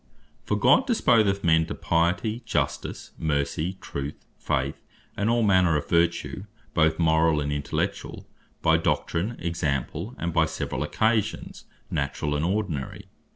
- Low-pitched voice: Yes, very low, 85 Hz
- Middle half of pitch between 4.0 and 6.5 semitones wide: Yes, average, 4.4 semitones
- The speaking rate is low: Yes, slow, 130 wpm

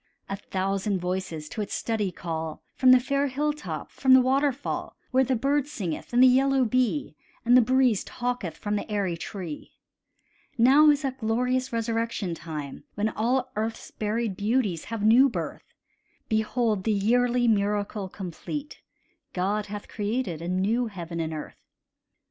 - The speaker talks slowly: No, average, 155 wpm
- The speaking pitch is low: No, high, 220 Hz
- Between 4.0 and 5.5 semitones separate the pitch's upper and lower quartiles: Yes, average, 4.8 semitones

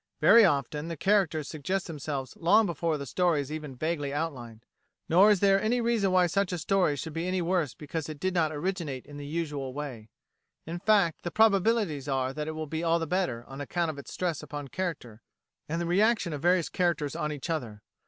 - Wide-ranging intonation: No, average, 4.1 semitones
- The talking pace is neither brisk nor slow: No, fast, 210 wpm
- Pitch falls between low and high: Yes, medium, 165 Hz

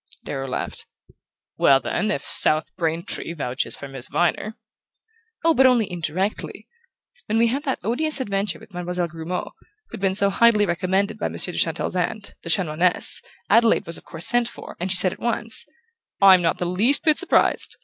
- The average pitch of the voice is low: No, high, 190 Hz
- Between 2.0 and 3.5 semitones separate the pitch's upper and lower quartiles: No, average, 5.2 semitones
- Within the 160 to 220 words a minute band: Yes, average, 180 wpm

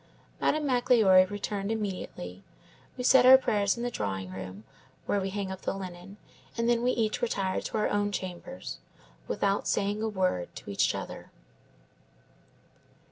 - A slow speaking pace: No, average, 155 wpm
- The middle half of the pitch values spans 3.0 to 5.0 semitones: Yes, average, 3.9 semitones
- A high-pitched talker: Yes, high, 200 Hz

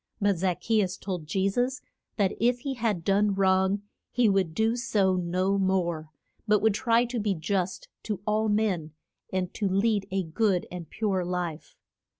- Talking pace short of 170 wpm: No, average, 175 wpm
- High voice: Yes, high, 195 Hz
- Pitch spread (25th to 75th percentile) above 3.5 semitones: No, average, 3.0 semitones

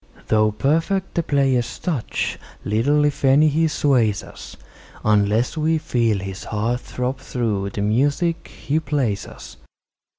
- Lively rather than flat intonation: Yes, wide, 5.7 semitones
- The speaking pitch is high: No, low, 130 Hz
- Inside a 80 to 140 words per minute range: Yes, slow, 135 wpm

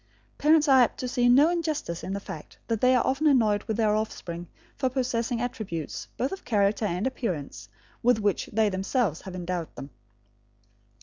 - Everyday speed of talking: Yes, average, 180 wpm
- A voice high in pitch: Yes, high, 225 Hz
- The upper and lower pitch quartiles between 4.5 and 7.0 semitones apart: Yes, average, 5.3 semitones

